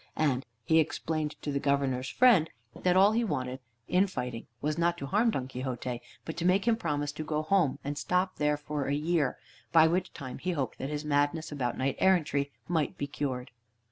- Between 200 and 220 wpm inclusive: Yes, fast, 205 wpm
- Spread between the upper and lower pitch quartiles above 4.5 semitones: No, average, 3.9 semitones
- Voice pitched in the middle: Yes, medium, 150 Hz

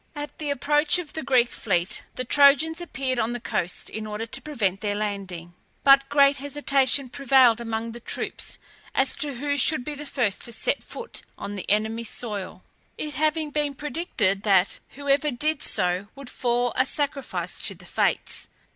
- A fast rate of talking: No, average, 175 wpm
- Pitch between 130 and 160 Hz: No, very high, 260 Hz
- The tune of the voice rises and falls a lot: No, average, 4.8 semitones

